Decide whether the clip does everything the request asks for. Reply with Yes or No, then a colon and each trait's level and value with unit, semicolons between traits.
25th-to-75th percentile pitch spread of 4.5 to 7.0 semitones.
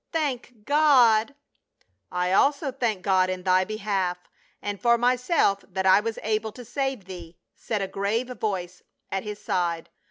Yes: average, 4.8 semitones